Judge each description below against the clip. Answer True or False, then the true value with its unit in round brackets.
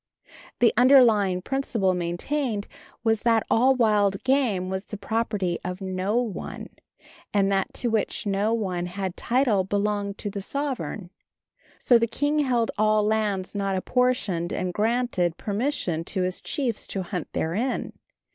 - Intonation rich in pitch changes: False (4.0 semitones)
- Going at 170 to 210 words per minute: False (145 wpm)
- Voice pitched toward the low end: False (210 Hz)